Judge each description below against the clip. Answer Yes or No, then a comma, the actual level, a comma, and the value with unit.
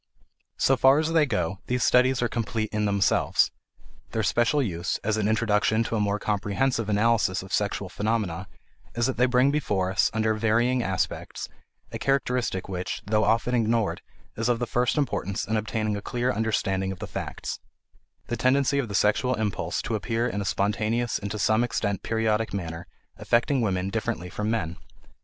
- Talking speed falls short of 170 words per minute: No, average, 180 wpm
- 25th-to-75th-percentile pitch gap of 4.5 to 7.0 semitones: No, average, 3.0 semitones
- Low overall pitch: Yes, low, 110 Hz